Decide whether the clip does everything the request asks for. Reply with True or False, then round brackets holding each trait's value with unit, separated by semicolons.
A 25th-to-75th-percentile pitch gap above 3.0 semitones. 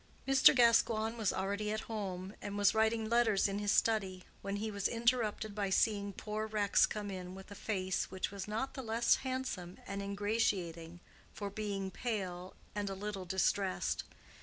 False (2.4 semitones)